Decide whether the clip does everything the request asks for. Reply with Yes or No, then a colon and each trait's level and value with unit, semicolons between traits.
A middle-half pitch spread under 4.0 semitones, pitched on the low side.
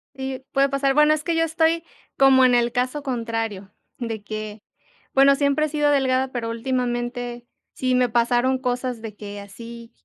No: average, 2.8 semitones; very high, 250 Hz